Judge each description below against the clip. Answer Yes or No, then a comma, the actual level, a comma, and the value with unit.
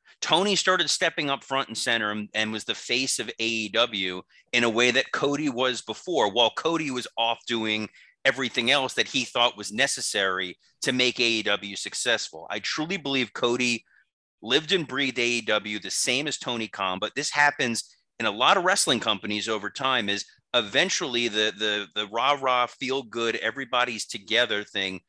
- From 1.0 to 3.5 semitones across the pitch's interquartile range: No, average, 3.9 semitones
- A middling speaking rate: Yes, average, 170 wpm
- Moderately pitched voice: No, low, 120 Hz